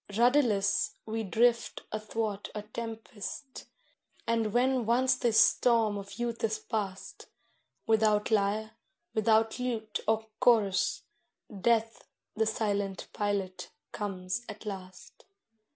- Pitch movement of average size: No, narrow, 2.2 semitones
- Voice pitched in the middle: No, high, 220 Hz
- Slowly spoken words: Yes, slow, 105 wpm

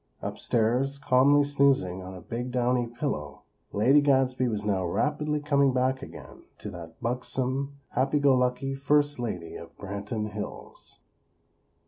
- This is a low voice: Yes, low, 125 Hz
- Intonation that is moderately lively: Yes, average, 4.6 semitones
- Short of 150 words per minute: Yes, slow, 135 wpm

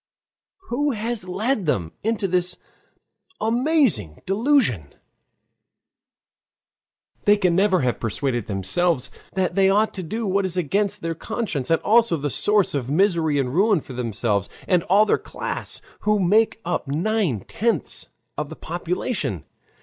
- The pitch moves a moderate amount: No, wide, 6.9 semitones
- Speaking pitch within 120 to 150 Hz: No, medium, 180 Hz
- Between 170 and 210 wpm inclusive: No, average, 140 wpm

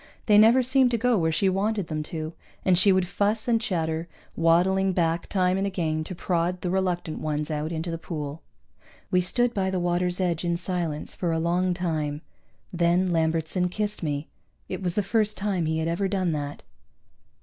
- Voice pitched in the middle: Yes, medium, 180 Hz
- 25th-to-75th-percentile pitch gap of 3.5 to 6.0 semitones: No, average, 3.0 semitones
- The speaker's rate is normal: Yes, average, 195 wpm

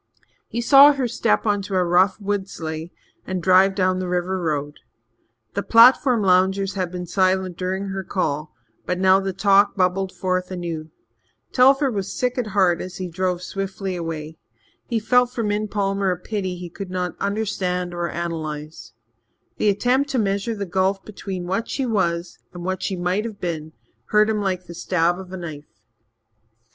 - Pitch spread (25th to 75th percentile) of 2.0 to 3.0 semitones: Yes, narrow, 2.4 semitones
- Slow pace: No, average, 175 wpm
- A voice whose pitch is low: No, high, 190 Hz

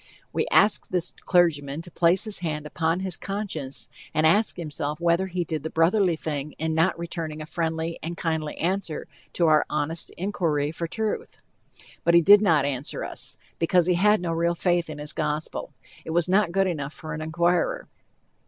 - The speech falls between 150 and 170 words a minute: No, average, 185 wpm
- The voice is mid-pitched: Yes, medium, 165 Hz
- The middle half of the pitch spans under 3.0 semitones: Yes, narrow, 2.4 semitones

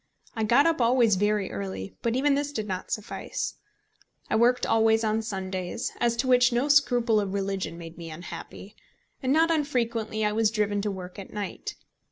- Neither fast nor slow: Yes, average, 185 wpm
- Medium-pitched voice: No, high, 220 Hz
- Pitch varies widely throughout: No, average, 3.9 semitones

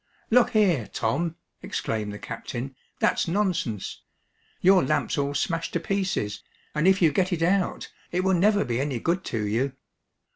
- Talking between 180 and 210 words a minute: No, average, 160 wpm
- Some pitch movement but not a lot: No, wide, 7.0 semitones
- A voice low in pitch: No, medium, 165 Hz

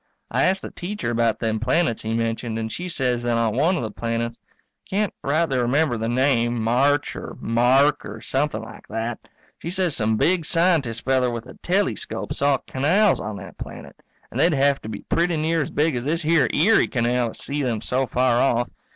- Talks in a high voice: No, low, 130 Hz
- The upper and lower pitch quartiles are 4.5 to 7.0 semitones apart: Yes, average, 5.3 semitones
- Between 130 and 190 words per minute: No, fast, 205 wpm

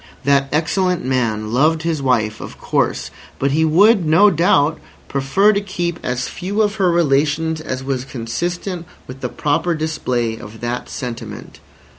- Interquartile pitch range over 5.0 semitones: Yes, wide, 5.4 semitones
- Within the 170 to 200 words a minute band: No, average, 155 wpm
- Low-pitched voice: No, medium, 150 Hz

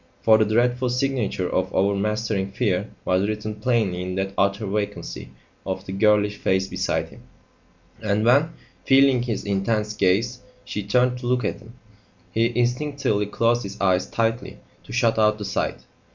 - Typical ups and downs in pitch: Yes, average, 3.5 semitones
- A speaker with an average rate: Yes, average, 160 wpm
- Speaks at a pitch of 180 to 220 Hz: No, low, 105 Hz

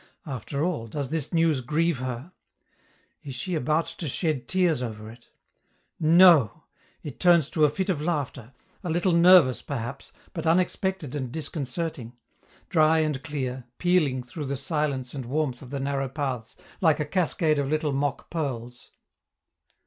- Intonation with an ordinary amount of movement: Yes, average, 4.1 semitones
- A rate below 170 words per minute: Yes, average, 155 wpm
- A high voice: No, medium, 150 Hz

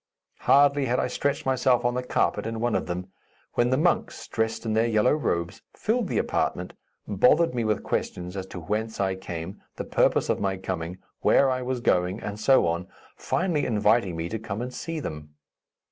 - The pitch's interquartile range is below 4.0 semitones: No, average, 5.3 semitones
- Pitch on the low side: Yes, low, 110 Hz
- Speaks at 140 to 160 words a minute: No, average, 195 wpm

